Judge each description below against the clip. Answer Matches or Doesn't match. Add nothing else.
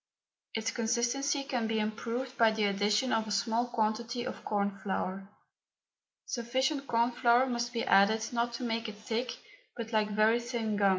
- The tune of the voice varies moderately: Doesn't match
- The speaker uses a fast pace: Doesn't match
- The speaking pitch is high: Matches